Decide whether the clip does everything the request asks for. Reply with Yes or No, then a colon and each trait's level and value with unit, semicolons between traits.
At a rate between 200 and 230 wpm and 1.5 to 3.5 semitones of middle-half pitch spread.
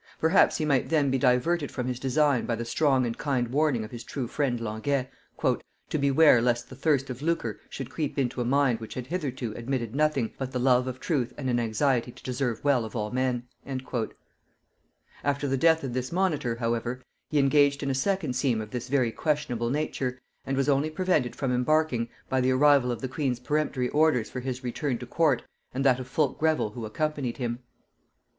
Yes: fast, 205 wpm; average, 3.0 semitones